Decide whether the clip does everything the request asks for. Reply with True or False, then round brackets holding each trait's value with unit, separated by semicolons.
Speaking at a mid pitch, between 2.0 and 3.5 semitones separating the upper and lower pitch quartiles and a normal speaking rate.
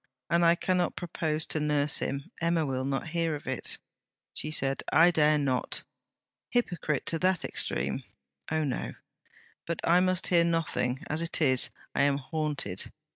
True (155 Hz; 3.0 semitones; 160 wpm)